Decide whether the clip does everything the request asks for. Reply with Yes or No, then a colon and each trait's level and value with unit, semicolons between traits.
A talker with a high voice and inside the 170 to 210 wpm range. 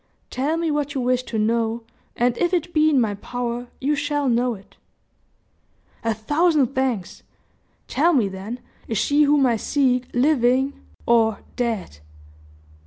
No: very high, 250 Hz; average, 150 wpm